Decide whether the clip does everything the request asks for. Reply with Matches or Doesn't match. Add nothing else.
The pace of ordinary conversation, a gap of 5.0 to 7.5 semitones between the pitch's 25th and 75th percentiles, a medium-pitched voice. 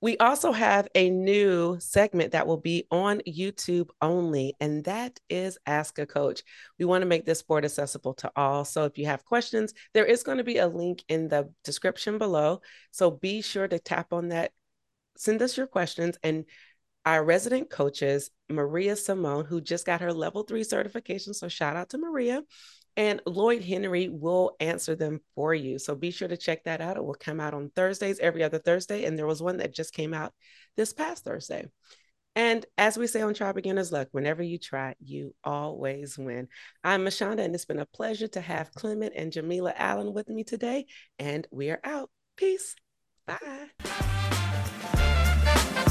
Matches